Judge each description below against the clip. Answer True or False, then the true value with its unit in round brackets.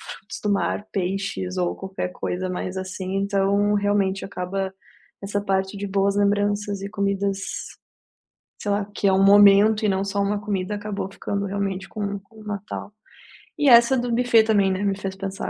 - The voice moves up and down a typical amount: False (1.1 semitones)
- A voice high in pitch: True (200 Hz)